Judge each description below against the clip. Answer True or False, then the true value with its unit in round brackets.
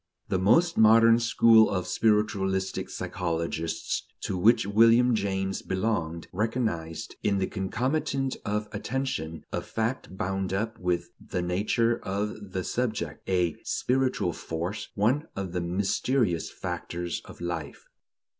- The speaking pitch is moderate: False (100 Hz)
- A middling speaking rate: False (125 wpm)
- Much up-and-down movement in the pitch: False (4.2 semitones)